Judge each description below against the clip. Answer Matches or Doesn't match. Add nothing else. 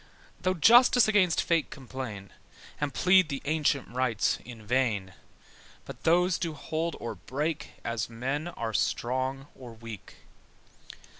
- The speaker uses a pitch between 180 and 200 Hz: Doesn't match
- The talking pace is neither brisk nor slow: Doesn't match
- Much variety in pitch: Matches